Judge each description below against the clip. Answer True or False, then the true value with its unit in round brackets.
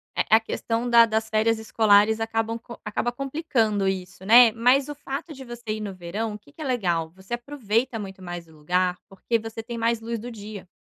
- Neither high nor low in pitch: False (225 Hz)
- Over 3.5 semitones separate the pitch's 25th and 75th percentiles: False (3.1 semitones)